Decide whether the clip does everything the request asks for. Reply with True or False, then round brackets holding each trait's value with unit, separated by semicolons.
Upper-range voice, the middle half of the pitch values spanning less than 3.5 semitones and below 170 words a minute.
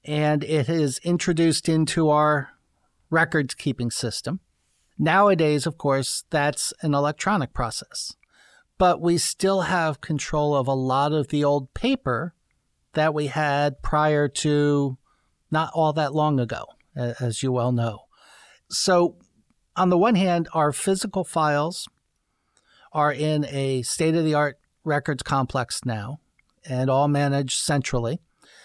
False (150 Hz; 2.9 semitones; 135 wpm)